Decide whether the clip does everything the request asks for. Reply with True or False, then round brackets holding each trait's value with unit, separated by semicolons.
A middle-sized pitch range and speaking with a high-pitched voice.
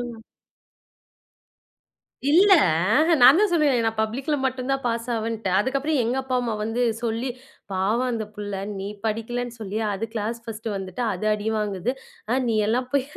True (3.2 semitones; 230 Hz)